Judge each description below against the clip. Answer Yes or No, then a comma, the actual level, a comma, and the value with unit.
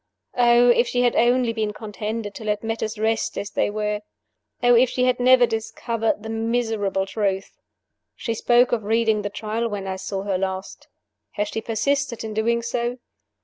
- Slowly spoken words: No, average, 180 wpm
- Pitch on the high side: Yes, high, 225 Hz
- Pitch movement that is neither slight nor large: No, narrow, 2.3 semitones